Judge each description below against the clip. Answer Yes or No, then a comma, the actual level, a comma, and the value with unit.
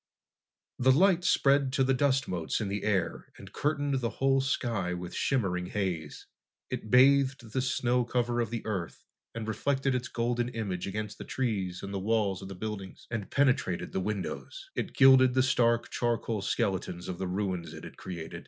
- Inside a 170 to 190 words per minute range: Yes, average, 180 wpm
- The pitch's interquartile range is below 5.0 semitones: No, average, 5.3 semitones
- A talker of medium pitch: No, low, 115 Hz